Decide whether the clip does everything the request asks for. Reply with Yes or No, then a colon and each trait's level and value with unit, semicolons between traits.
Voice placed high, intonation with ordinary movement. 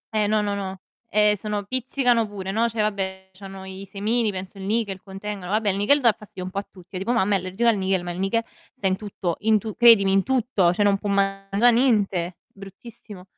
No: high, 200 Hz; narrow, 2.3 semitones